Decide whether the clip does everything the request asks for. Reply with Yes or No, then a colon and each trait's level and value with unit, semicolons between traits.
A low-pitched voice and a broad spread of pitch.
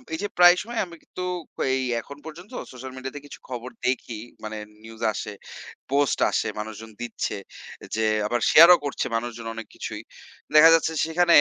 Yes: low, 130 Hz; wide, 6.2 semitones